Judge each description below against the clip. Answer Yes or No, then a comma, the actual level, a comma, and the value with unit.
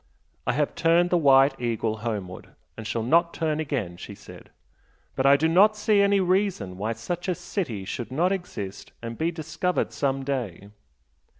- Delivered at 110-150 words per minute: No, average, 175 wpm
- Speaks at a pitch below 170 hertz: Yes, medium, 140 Hz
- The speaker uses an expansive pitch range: Yes, wide, 7.7 semitones